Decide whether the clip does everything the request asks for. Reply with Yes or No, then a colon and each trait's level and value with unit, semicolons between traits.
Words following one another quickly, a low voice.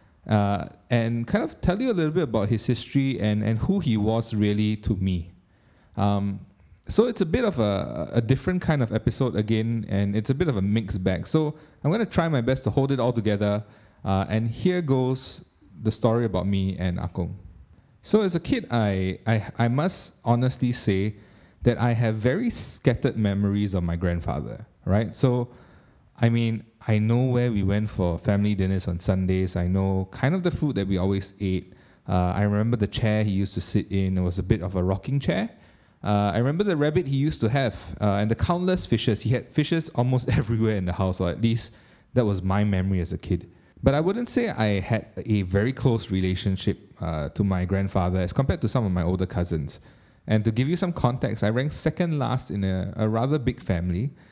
Yes: fast, 215 wpm; low, 110 Hz